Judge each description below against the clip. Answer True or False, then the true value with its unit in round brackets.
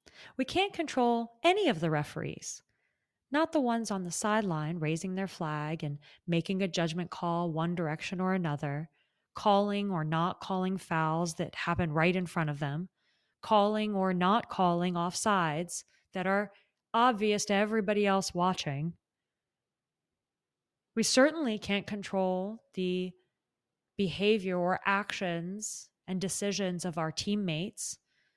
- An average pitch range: True (3.4 semitones)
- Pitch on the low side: False (185 Hz)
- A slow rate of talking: True (130 wpm)